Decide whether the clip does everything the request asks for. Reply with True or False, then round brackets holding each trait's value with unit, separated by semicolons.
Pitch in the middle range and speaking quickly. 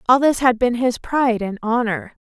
False (240 Hz; 215 wpm)